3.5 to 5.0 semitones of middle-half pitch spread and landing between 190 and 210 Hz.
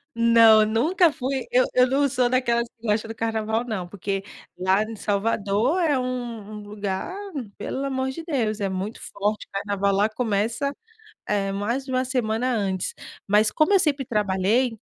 No: average, 3.8 semitones; high, 225 Hz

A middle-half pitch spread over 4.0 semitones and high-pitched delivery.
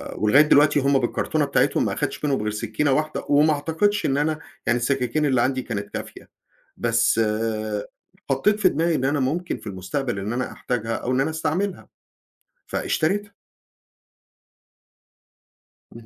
No: average, 4.6 semitones; medium, 140 Hz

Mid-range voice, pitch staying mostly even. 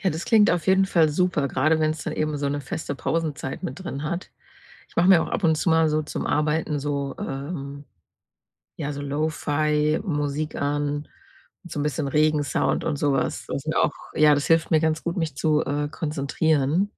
Yes: medium, 150 Hz; narrow, 2.0 semitones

